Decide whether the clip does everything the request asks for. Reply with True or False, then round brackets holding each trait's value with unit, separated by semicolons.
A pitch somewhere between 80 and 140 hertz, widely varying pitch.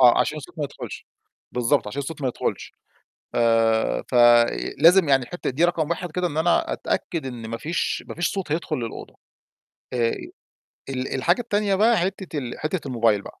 False (150 Hz; 5.9 semitones)